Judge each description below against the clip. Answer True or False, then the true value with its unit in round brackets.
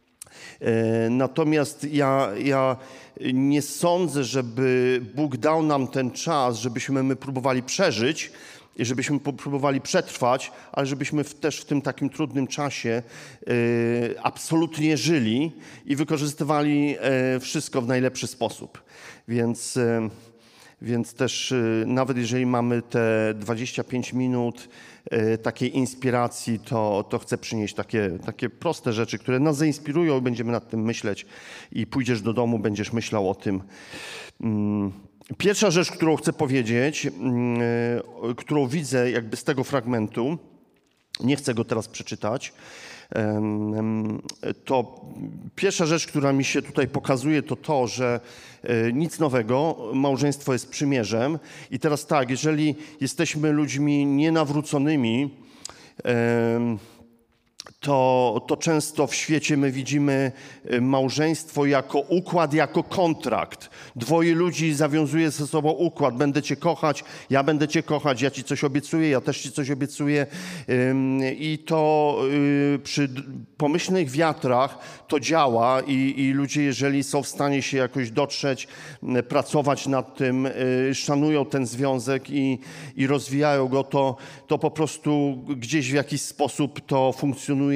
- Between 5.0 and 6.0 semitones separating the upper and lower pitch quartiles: False (3.4 semitones)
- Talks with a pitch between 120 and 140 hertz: True (135 Hz)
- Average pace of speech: True (120 wpm)